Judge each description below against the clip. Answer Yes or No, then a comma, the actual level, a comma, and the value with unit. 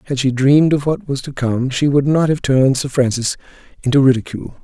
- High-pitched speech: No, low, 135 Hz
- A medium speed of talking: No, fast, 220 wpm